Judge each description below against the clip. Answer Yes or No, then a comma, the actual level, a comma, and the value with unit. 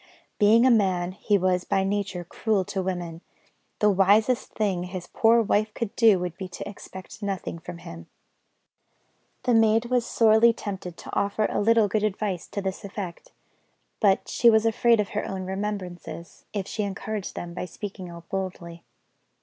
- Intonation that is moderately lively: Yes, average, 3.0 semitones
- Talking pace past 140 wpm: Yes, average, 170 wpm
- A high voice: Yes, high, 200 Hz